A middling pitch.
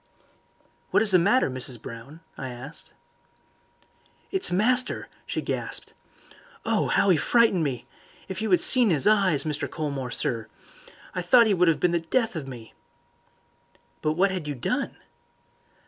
Yes: medium, 170 Hz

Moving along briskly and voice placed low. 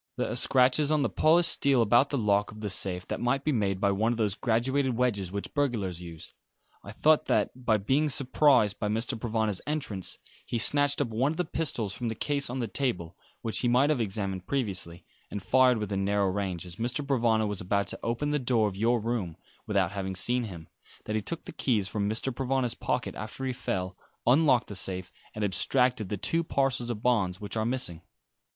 Yes: fast, 210 wpm; low, 115 Hz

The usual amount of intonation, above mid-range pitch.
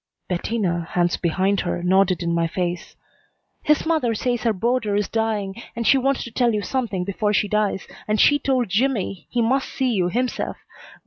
Yes: average, 4.8 semitones; high, 210 Hz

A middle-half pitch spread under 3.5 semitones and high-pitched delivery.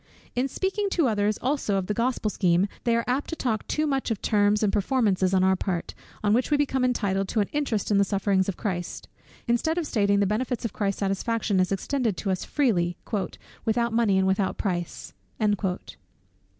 No: average, 4.3 semitones; high, 210 Hz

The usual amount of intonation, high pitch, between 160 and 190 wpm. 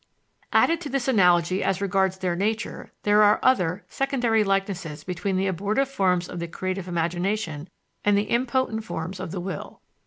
Yes: average, 3.4 semitones; high, 195 Hz; average, 165 wpm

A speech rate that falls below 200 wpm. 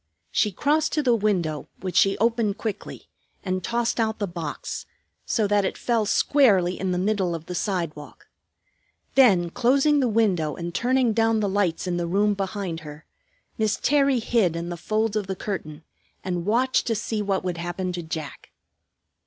Yes: average, 180 wpm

